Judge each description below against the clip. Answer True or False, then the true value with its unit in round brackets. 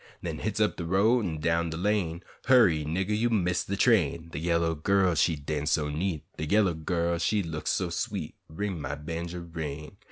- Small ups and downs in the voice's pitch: False (3.6 semitones)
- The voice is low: True (85 Hz)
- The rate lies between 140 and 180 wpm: False (195 wpm)